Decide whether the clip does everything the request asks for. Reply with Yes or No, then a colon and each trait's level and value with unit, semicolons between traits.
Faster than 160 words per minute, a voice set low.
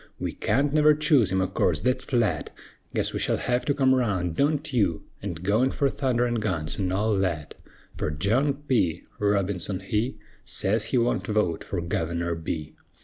Yes: average, 185 wpm; low, 105 Hz